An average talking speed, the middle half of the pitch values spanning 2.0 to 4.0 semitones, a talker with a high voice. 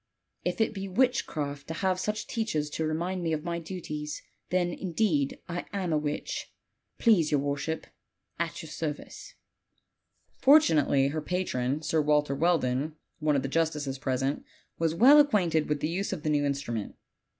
No: average, 160 wpm; average, 3.7 semitones; medium, 160 Hz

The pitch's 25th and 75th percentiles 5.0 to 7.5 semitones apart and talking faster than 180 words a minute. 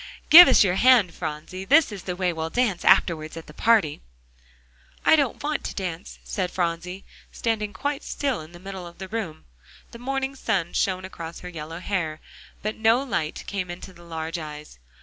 Yes: average, 5.3 semitones; average, 190 wpm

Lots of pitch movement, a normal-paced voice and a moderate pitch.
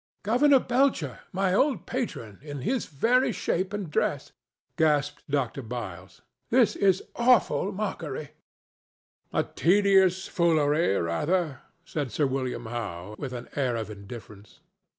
No: wide, 8.3 semitones; slow, 120 wpm; medium, 150 Hz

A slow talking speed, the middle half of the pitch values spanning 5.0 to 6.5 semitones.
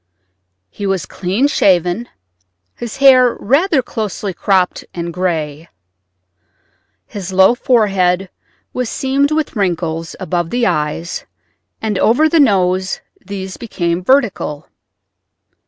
Yes: slow, 105 wpm; average, 5.3 semitones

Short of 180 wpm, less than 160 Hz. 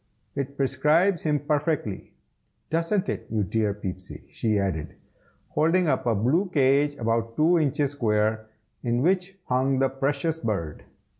Yes: average, 140 wpm; low, 135 Hz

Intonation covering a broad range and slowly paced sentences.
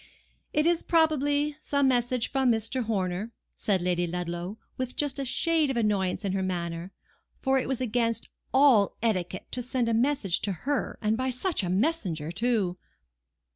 No: wide, 6.2 semitones; average, 170 wpm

